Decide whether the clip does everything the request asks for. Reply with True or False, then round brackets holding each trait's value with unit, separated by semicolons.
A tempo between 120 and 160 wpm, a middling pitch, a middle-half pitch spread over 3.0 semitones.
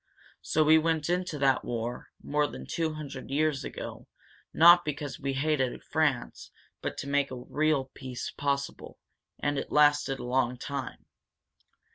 False (150 wpm; 145 Hz; 2.6 semitones)